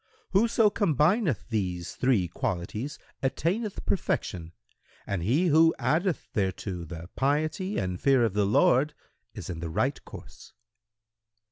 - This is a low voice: Yes, low, 130 Hz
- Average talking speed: No, slow, 125 wpm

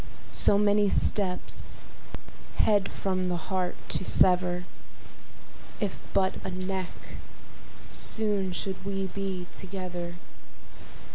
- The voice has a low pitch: No, high, 190 Hz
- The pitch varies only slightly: Yes, narrow, 1.6 semitones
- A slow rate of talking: Yes, slow, 95 wpm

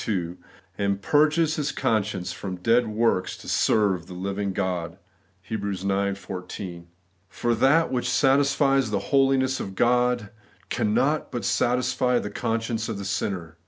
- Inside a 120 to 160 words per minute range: Yes, average, 140 wpm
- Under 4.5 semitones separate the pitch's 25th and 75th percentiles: No, average, 4.8 semitones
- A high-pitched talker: No, low, 110 Hz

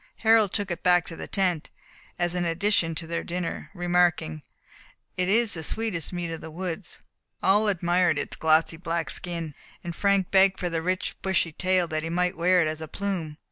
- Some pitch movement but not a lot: No, narrow, 2.3 semitones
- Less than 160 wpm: No, average, 195 wpm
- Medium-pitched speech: Yes, medium, 175 Hz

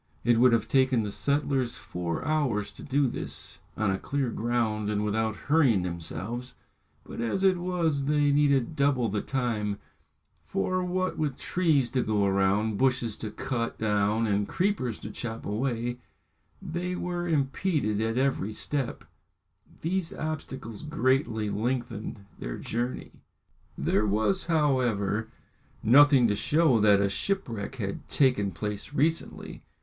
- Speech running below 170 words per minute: Yes, average, 140 wpm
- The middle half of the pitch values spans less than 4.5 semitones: No, average, 5.3 semitones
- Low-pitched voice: Yes, low, 120 Hz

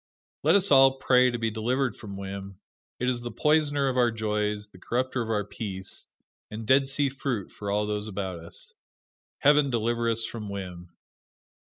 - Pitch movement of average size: Yes, average, 4.1 semitones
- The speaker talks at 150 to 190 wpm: Yes, average, 180 wpm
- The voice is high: No, low, 115 Hz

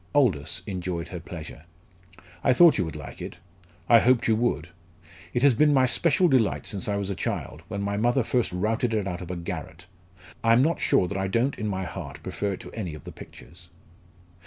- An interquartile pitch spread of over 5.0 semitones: Yes, wide, 5.4 semitones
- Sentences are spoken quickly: Yes, fast, 215 wpm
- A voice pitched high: No, low, 100 Hz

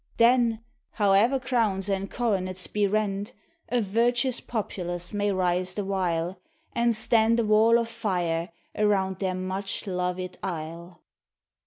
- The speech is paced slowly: Yes, slow, 130 wpm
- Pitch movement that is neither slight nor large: Yes, average, 3.6 semitones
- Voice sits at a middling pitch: No, high, 195 Hz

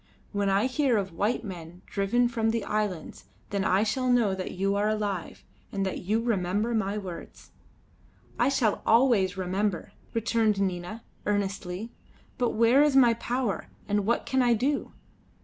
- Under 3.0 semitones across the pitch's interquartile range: No, average, 3.4 semitones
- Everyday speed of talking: Yes, average, 160 wpm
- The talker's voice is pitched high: Yes, high, 210 Hz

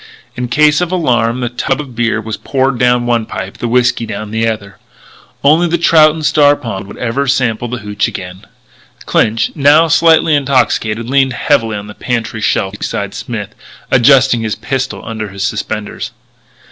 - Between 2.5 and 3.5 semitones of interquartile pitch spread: No, average, 4.2 semitones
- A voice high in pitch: No, low, 120 Hz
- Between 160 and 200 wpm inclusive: Yes, average, 170 wpm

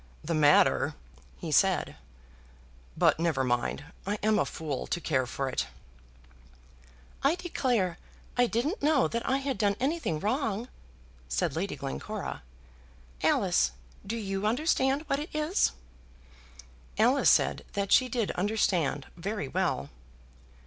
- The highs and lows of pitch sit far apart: Yes, wide, 8.8 semitones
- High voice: Yes, high, 210 Hz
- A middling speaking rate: No, slow, 130 wpm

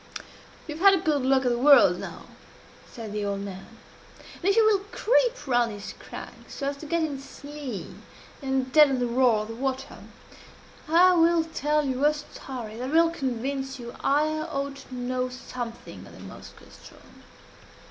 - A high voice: Yes, very high, 275 Hz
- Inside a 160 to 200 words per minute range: Yes, average, 185 wpm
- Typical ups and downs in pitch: Yes, average, 3.8 semitones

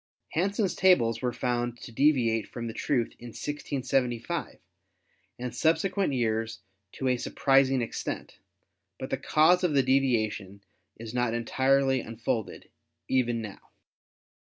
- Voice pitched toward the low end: Yes, low, 125 Hz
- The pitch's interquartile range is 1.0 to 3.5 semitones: Yes, average, 3.1 semitones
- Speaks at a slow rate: Yes, slow, 130 wpm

